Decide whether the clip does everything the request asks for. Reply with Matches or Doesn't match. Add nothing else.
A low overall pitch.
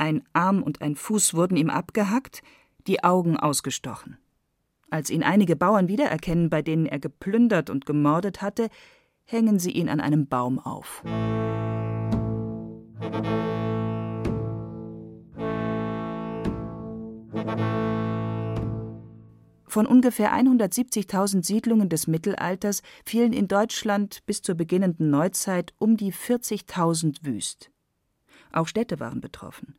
Doesn't match